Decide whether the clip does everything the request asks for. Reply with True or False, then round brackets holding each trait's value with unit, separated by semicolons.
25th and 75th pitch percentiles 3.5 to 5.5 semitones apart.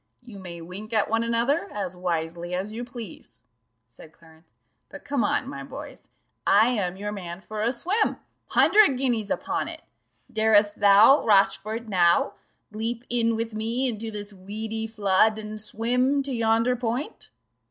False (3.1 semitones)